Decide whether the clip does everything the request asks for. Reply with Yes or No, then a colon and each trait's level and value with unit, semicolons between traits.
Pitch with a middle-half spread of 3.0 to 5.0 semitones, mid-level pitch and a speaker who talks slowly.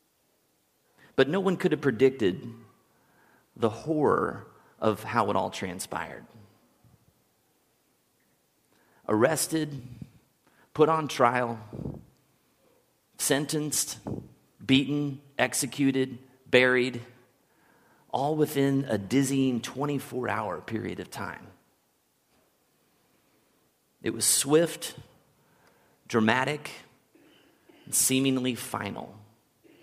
No: average, 3.8 semitones; low, 130 Hz; slow, 75 wpm